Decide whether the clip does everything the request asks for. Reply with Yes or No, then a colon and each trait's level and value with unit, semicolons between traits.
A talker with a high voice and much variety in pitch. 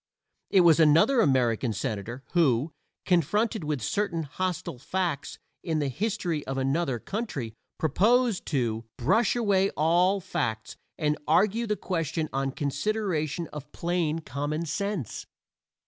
No: medium, 160 Hz; wide, 5.7 semitones